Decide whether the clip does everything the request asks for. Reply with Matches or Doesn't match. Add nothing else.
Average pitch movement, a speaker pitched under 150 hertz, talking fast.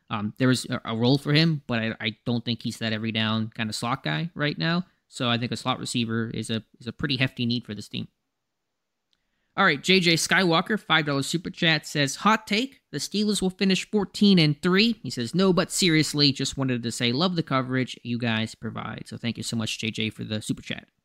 Doesn't match